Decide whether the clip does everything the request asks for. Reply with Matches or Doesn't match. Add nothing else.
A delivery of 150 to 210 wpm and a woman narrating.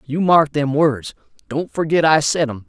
Doesn't match